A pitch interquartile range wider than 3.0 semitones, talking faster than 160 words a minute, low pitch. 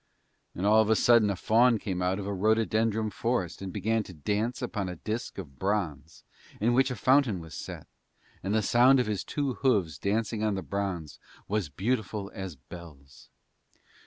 Yes: average, 3.7 semitones; average, 185 wpm; low, 105 Hz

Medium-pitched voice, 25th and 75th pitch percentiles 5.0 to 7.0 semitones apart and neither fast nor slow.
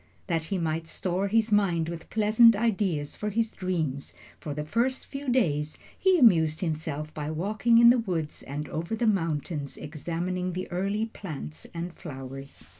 Yes: medium, 175 Hz; wide, 5.6 semitones; average, 165 wpm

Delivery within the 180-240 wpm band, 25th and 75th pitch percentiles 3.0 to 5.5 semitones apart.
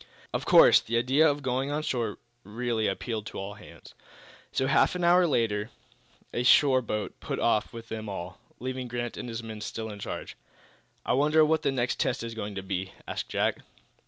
Yes: average, 195 wpm; average, 3.8 semitones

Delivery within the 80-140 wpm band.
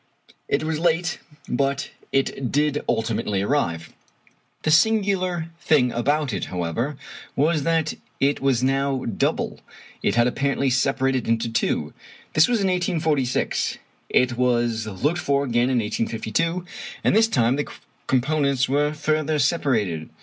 Yes: slow, 135 wpm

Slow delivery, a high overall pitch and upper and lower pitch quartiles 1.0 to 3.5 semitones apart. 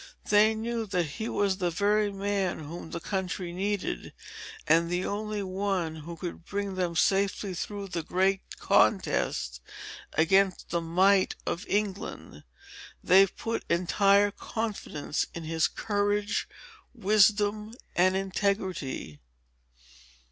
Yes: slow, 120 wpm; high, 195 Hz; average, 2.8 semitones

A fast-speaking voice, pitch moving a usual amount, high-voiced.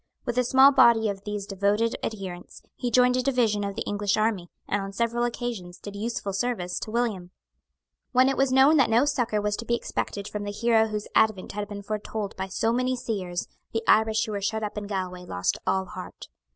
Yes: fast, 215 wpm; average, 3.0 semitones; high, 215 Hz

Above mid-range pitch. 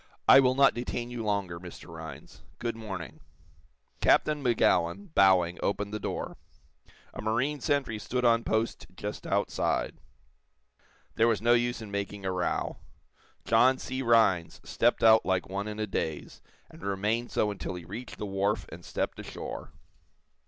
No: low, 105 Hz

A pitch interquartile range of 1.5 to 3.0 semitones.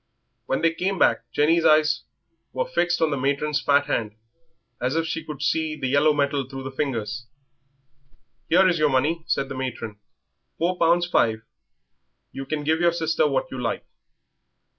No: average, 3.5 semitones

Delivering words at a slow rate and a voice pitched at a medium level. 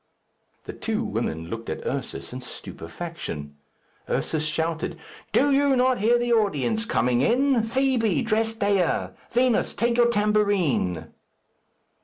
No: slow, 125 wpm; high, 210 Hz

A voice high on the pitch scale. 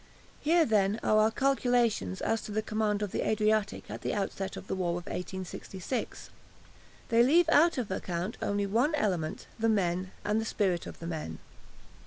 Yes: high, 210 Hz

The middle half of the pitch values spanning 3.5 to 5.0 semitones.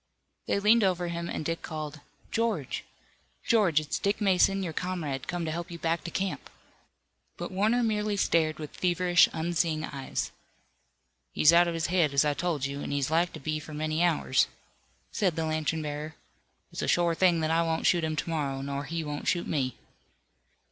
No: narrow, 2.5 semitones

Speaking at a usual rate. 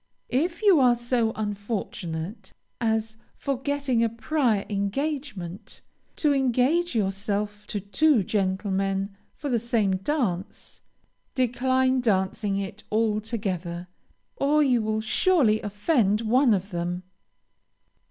No: slow, 105 wpm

